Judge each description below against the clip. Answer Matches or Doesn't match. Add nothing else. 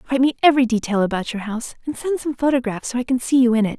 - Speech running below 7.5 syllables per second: Doesn't match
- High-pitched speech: Matches